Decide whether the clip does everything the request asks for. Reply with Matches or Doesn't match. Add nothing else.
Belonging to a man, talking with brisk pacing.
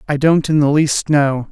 Matches